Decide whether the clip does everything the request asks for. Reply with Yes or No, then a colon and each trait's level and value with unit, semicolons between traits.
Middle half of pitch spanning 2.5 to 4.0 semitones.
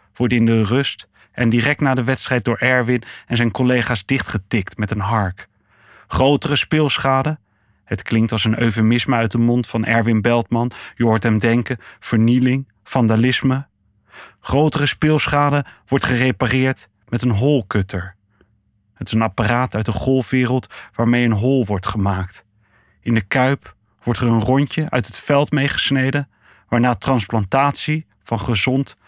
Yes: average, 3.3 semitones